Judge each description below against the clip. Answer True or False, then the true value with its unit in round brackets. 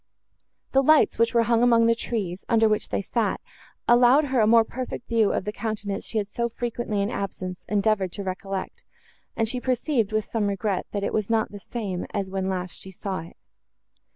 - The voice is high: True (215 Hz)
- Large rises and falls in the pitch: False (3.0 semitones)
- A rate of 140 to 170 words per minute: False (205 wpm)